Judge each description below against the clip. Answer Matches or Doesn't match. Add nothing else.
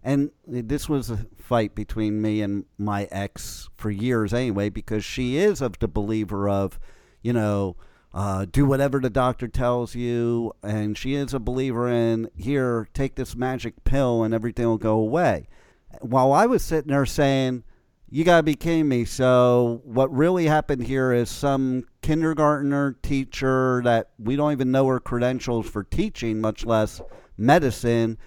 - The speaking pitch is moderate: Doesn't match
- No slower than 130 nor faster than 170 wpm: Matches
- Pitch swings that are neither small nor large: Matches